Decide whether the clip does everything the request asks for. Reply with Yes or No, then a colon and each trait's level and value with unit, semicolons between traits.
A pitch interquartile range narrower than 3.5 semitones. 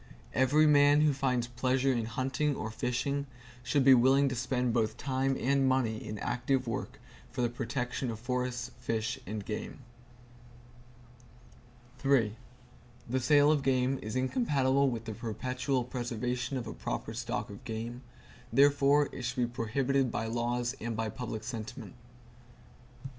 Yes: narrow, 2.4 semitones